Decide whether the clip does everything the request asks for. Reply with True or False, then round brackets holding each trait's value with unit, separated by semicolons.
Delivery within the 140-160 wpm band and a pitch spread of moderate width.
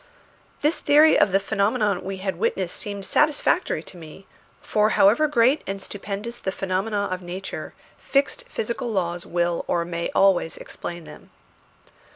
True (150 wpm; 4.3 semitones)